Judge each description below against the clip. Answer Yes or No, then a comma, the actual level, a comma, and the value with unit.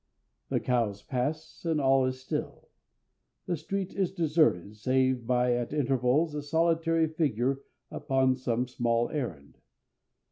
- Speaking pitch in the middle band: No, low, 130 Hz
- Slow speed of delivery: Yes, slow, 130 wpm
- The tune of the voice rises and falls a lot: No, average, 4.3 semitones